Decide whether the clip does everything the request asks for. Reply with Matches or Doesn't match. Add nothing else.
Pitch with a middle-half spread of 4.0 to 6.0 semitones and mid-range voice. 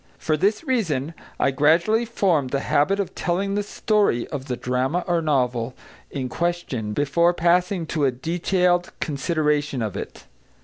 Matches